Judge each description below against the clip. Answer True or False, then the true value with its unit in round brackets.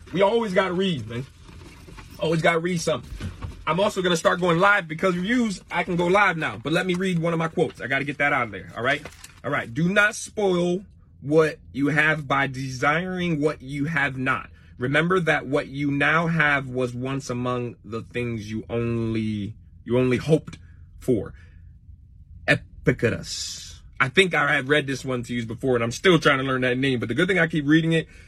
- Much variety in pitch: True (6.4 semitones)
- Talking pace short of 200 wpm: False (205 wpm)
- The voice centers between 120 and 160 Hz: True (140 Hz)